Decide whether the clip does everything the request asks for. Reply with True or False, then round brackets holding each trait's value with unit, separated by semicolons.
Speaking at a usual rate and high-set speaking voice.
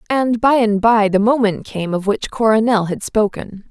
True (195 wpm; 215 Hz)